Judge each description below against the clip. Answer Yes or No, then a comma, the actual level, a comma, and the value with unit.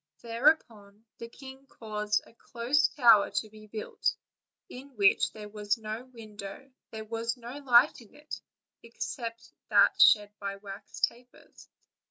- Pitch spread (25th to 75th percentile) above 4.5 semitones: No, average, 2.9 semitones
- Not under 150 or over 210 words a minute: No, average, 140 wpm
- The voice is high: Yes, high, 230 Hz